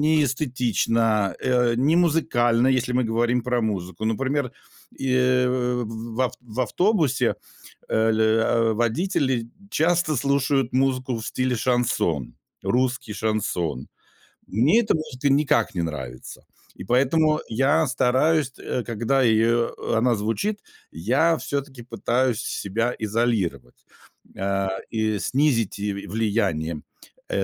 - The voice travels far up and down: No, average, 3.4 semitones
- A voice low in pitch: Yes, low, 120 Hz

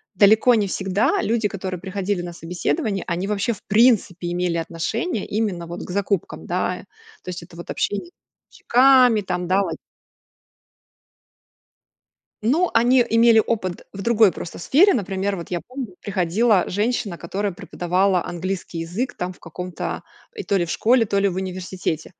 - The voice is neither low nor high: No, high, 195 Hz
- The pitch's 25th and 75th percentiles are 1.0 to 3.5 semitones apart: No, average, 4.0 semitones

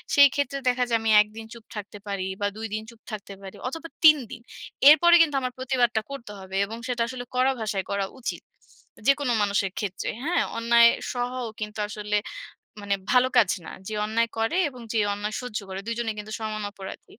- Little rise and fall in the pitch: No, average, 3.4 semitones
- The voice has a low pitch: No, high, 230 Hz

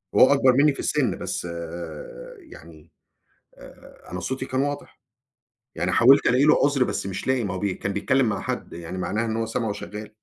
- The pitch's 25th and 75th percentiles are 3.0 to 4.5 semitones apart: No, average, 5.2 semitones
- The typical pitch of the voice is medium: No, low, 115 Hz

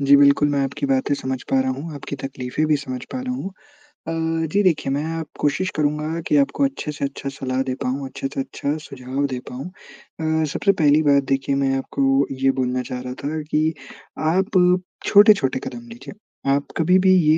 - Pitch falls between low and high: Yes, medium, 145 Hz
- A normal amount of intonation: Yes, average, 3.2 semitones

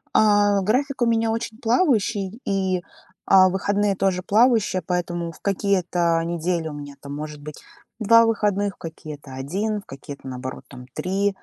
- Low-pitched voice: No, high, 190 Hz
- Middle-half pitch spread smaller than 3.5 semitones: No, average, 4.3 semitones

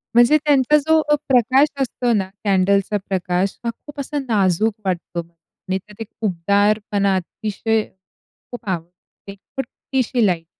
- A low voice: No, high, 210 Hz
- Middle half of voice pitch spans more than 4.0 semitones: Yes, average, 4.6 semitones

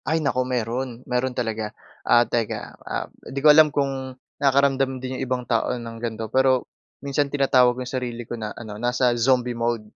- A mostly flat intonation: Yes, narrow, 2.1 semitones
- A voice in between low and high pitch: No, low, 125 Hz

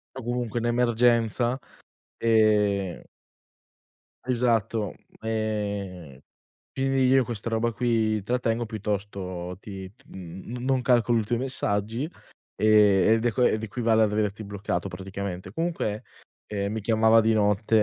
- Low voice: Yes, low, 110 Hz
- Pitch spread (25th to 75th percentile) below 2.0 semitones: No, average, 2.7 semitones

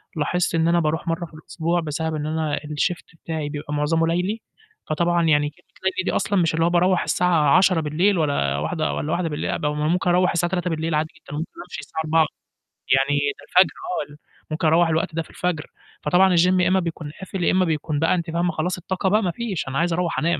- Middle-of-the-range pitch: Yes, medium, 165 Hz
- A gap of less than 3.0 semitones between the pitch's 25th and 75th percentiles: Yes, narrow, 2.5 semitones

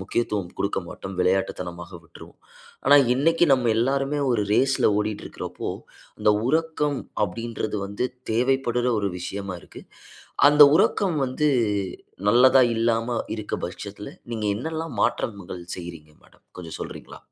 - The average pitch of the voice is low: Yes, low, 115 Hz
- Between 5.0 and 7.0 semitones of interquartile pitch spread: Yes, wide, 5.5 semitones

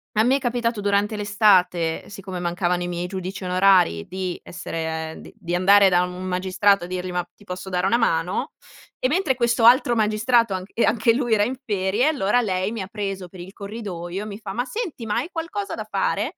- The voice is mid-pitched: No, high, 200 Hz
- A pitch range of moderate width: Yes, average, 3.8 semitones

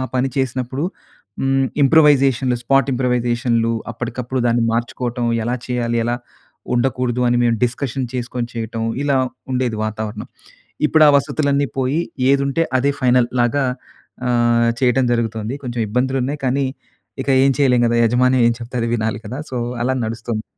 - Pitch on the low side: Yes, low, 125 Hz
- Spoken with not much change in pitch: Yes, narrow, 2.1 semitones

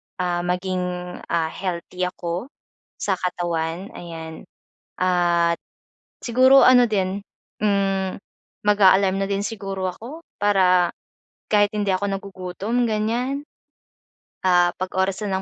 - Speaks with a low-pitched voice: No, high, 190 Hz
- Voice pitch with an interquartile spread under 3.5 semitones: Yes, narrow, 2.5 semitones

